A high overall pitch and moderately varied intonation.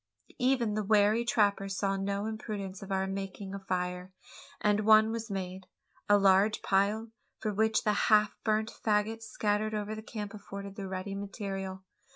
No: high, 205 Hz; narrow, 1.9 semitones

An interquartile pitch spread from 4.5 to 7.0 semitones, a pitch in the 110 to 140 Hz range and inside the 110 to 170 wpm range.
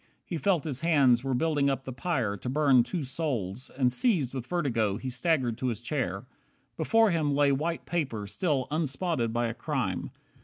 No: average, 4.8 semitones; low, 135 Hz; average, 185 wpm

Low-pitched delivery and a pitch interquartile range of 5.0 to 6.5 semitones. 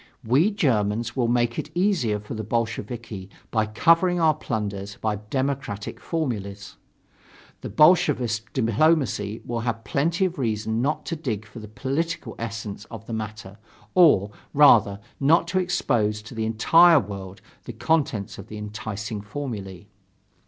Yes: low, 115 Hz; wide, 5.6 semitones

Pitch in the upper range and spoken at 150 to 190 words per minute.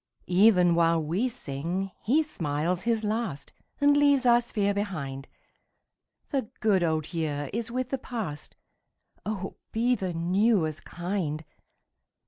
No: high, 195 Hz; slow, 135 wpm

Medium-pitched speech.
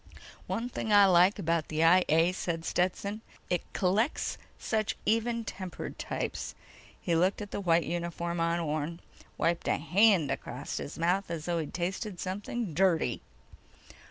Yes: medium, 180 Hz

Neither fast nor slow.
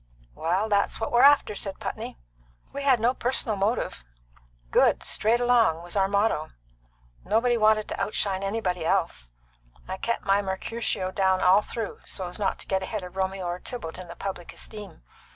Yes: average, 175 wpm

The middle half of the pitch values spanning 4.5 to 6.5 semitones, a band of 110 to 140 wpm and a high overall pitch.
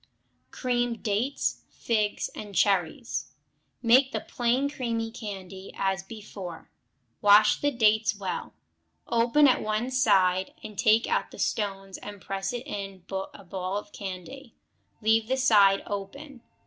No: average, 3.7 semitones; slow, 135 wpm; high, 215 Hz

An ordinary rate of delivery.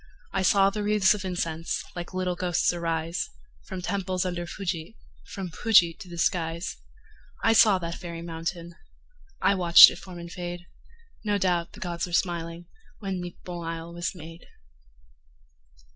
Yes: average, 155 wpm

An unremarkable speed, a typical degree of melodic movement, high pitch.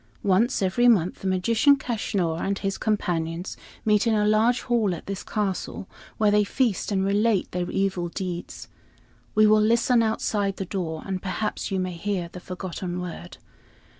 Yes: average, 165 wpm; average, 3.0 semitones; high, 195 Hz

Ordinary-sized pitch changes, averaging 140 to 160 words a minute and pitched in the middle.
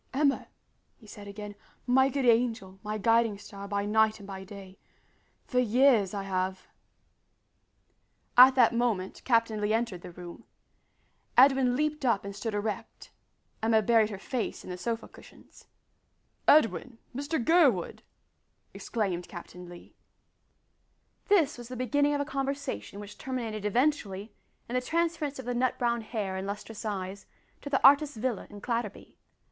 No: average, 4.3 semitones; average, 150 wpm; high, 225 Hz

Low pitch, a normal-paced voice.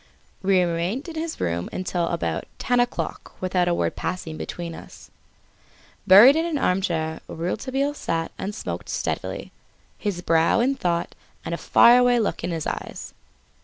No: medium, 185 Hz; average, 160 wpm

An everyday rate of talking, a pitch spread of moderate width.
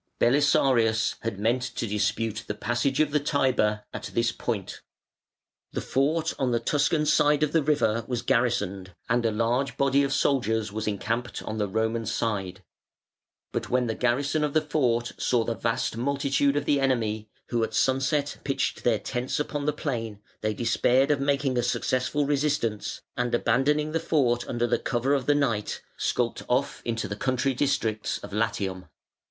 Yes: average, 170 wpm; average, 3.9 semitones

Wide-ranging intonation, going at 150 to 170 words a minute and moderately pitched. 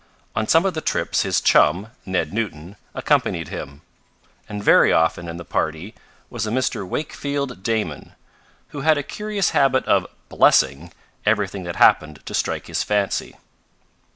No: wide, 7.9 semitones; average, 155 wpm; low, 105 Hz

